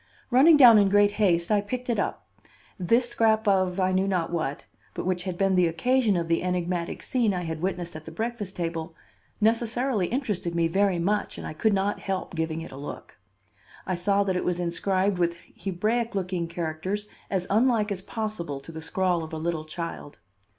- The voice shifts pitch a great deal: No, average, 3.7 semitones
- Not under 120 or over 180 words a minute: No, average, 200 wpm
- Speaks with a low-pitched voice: No, medium, 185 Hz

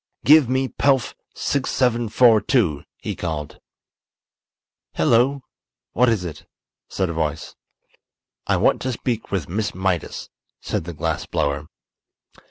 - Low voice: Yes, low, 105 Hz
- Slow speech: Yes, slow, 115 wpm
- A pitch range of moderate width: No, wide, 7.6 semitones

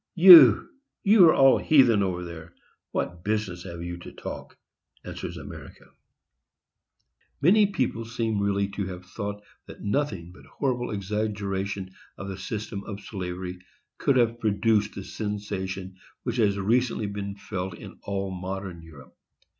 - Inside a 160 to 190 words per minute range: No, average, 140 wpm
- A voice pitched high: No, low, 100 Hz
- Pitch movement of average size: Yes, average, 3.4 semitones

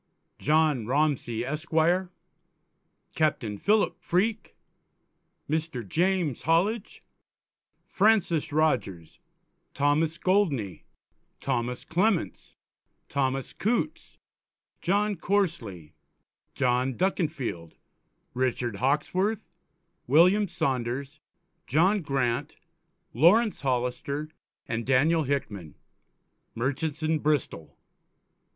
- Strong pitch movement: Yes, wide, 6.0 semitones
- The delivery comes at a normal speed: No, slow, 75 wpm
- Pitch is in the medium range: Yes, medium, 150 Hz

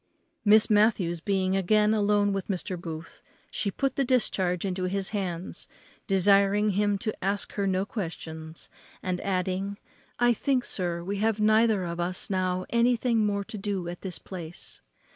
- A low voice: No, high, 195 Hz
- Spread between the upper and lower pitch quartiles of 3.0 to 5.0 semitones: No, narrow, 2.6 semitones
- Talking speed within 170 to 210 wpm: No, average, 160 wpm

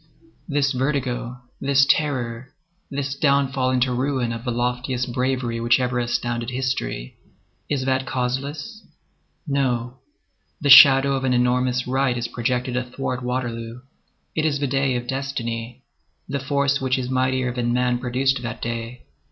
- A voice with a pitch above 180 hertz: No, low, 130 Hz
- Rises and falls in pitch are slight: Yes, narrow, 1.8 semitones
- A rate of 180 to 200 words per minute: No, average, 140 wpm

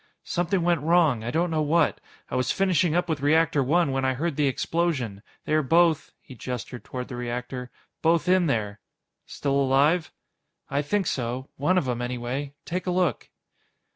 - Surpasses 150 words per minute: Yes, average, 180 wpm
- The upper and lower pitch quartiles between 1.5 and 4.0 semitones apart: No, average, 5.0 semitones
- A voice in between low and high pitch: Yes, medium, 145 Hz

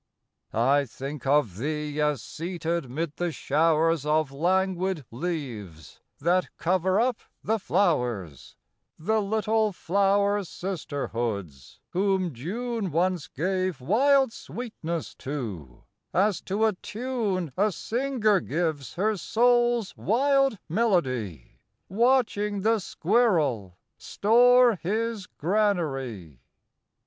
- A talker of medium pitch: Yes, medium, 180 Hz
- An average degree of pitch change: No, wide, 7.0 semitones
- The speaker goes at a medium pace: No, slow, 100 wpm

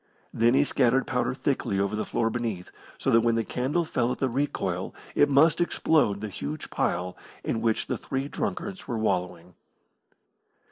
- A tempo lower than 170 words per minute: No, average, 175 wpm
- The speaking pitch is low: Yes, low, 120 Hz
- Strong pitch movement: No, average, 4.8 semitones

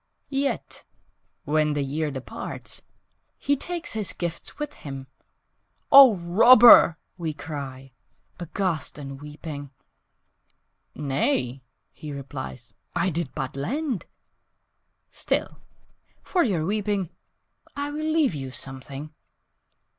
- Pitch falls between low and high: Yes, medium, 160 Hz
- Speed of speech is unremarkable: No, slow, 100 wpm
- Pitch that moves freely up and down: Yes, wide, 8.0 semitones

